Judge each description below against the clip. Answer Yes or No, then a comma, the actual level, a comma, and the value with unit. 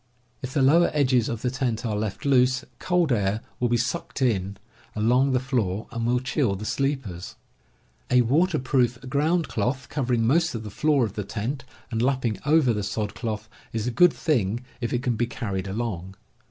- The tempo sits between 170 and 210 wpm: Yes, average, 195 wpm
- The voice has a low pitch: Yes, low, 120 Hz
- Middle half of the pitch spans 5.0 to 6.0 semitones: No, average, 3.8 semitones